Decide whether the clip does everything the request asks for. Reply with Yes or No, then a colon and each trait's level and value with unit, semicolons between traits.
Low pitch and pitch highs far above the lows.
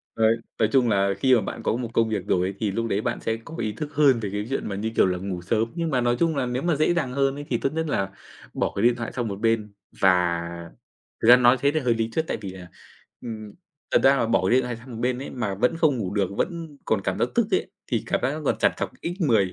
No: low, 115 Hz; average, 4.7 semitones